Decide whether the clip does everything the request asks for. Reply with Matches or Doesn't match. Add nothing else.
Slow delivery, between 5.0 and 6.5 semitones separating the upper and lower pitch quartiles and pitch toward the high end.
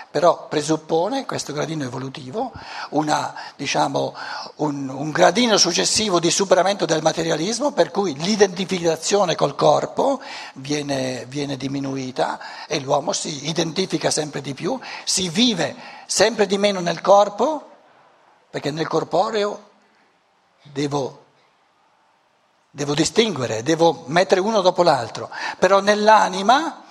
Doesn't match